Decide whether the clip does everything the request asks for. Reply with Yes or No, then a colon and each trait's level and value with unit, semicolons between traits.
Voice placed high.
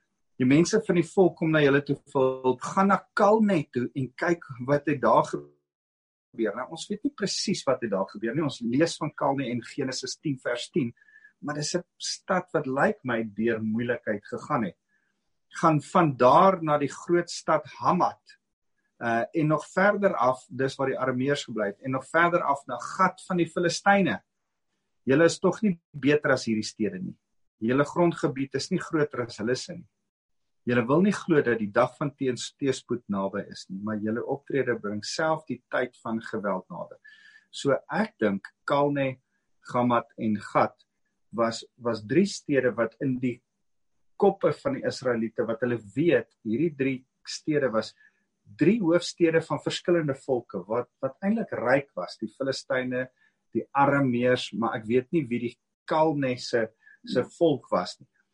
No: low, 135 Hz